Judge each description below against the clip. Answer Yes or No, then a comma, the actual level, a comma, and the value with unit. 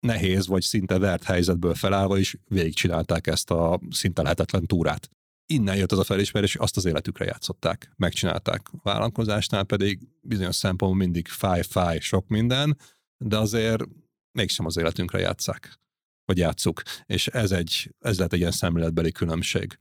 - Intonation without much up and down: No, average, 3.7 semitones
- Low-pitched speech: Yes, very low, 95 Hz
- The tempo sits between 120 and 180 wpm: Yes, average, 150 wpm